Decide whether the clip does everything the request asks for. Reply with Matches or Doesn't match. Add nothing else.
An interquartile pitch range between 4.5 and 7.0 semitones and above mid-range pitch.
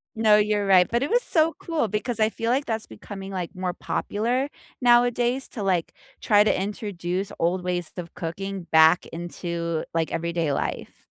Matches